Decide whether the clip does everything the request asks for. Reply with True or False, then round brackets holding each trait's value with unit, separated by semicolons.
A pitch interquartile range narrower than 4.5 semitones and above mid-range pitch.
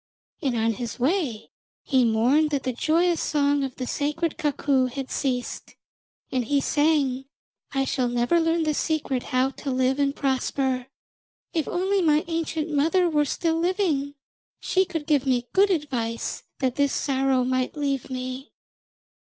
True (3.6 semitones; 280 Hz)